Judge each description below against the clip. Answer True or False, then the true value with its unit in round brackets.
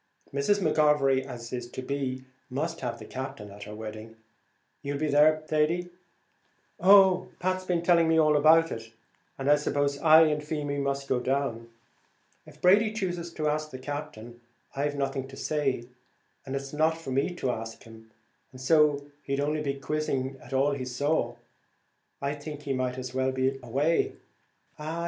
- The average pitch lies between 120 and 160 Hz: True (140 Hz)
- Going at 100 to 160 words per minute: False (170 wpm)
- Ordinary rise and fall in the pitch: True (3.0 semitones)